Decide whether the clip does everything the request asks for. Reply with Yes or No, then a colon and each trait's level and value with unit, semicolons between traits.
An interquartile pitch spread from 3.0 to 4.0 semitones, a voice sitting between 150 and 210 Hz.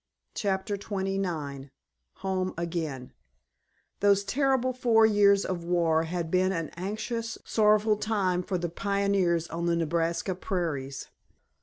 Yes: average, 3.3 semitones; medium, 185 Hz